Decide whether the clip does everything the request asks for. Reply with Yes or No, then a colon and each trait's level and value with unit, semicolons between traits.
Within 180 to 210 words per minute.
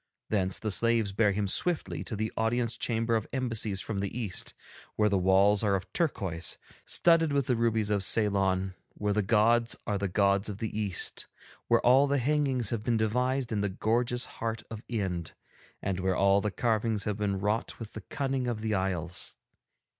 Yes: average, 190 wpm